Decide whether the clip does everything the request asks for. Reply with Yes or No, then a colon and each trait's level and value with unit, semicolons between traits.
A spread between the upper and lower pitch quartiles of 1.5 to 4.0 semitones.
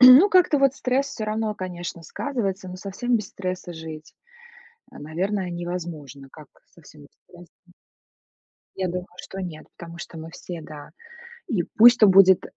No: average, 4.5 semitones